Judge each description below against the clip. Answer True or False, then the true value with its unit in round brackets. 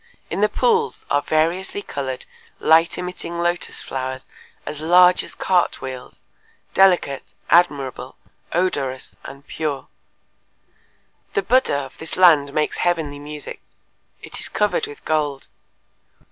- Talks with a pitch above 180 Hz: False (155 Hz)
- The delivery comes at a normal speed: False (120 wpm)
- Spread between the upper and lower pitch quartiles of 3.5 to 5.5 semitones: True (4.1 semitones)